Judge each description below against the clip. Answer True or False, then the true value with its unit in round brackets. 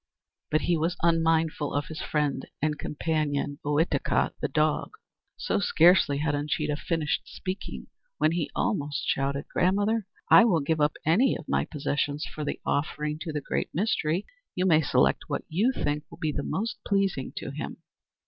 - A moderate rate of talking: True (165 wpm)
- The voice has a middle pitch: True (155 Hz)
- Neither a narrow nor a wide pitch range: True (3.1 semitones)